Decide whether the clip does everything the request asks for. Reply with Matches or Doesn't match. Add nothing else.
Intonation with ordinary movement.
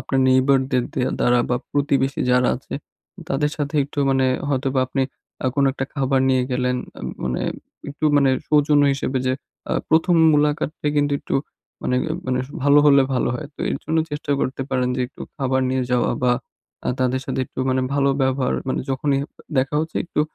Doesn't match